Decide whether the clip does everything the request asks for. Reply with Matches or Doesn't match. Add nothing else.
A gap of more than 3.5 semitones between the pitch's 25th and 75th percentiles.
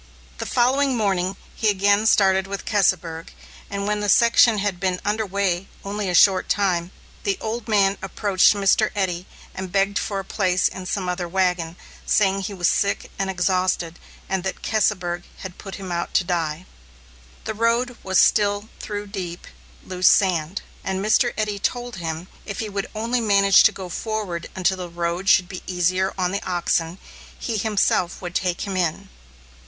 Doesn't match